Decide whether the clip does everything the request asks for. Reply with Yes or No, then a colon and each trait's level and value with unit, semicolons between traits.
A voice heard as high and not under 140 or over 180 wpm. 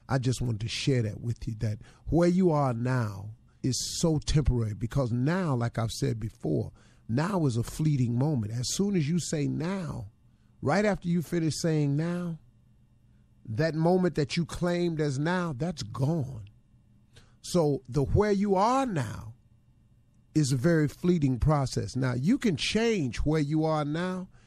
No: medium, 140 Hz; average, 165 wpm